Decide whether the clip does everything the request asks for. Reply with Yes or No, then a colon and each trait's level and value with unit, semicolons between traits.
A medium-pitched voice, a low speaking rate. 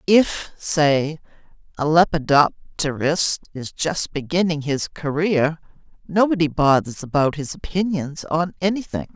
Yes: medium, 160 Hz; slow, 105 wpm